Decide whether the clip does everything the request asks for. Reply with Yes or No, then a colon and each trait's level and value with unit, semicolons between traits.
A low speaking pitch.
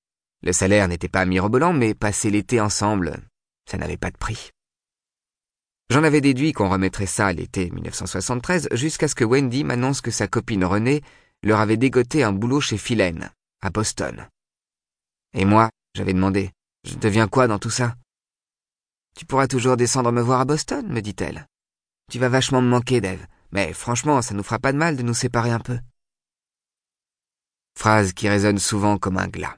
Yes: low, 110 Hz